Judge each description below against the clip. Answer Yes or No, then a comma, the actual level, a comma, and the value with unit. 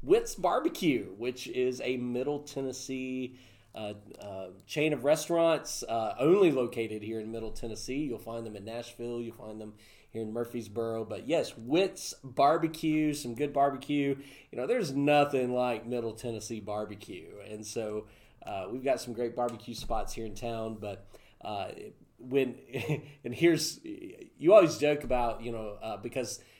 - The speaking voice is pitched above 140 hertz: No, low, 120 Hz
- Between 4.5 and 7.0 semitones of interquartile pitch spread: No, average, 4.1 semitones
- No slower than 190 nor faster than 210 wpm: No, average, 160 wpm